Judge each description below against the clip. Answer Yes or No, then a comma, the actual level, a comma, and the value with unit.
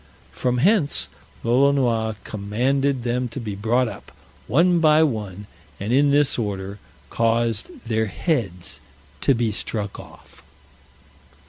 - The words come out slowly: Yes, slow, 120 wpm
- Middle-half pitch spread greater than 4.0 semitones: Yes, average, 4.6 semitones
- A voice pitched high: No, low, 120 Hz